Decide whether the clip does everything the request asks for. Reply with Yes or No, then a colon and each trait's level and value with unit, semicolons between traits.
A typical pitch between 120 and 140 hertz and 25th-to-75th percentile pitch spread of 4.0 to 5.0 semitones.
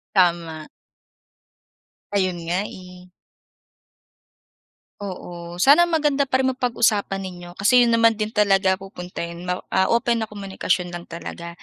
No: high, 195 Hz; average, 4.4 semitones